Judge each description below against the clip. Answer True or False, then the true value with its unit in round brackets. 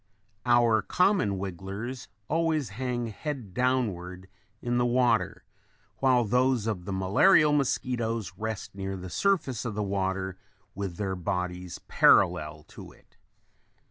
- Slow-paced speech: True (125 wpm)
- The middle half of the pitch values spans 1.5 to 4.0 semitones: False (4.9 semitones)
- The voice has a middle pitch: False (110 Hz)